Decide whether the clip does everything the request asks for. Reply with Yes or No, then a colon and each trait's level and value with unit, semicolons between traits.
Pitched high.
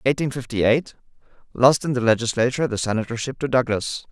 No: low, 125 Hz